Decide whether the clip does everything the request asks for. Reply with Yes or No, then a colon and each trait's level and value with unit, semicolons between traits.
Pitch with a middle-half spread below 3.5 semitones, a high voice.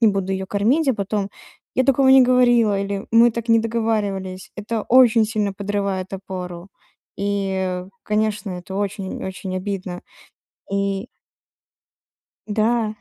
Yes: average, 2.9 semitones; high, 205 Hz